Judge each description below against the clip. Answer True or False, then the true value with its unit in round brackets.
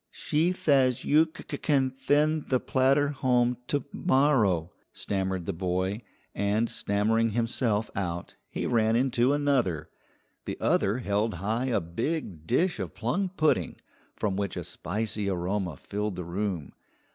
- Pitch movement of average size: False (5.7 semitones)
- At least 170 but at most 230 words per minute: False (145 wpm)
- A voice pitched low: True (115 Hz)